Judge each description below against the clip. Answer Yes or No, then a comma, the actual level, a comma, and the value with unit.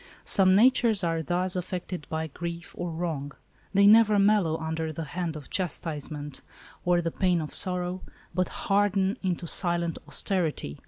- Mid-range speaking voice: Yes, medium, 175 Hz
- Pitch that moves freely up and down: No, average, 2.8 semitones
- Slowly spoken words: No, average, 155 wpm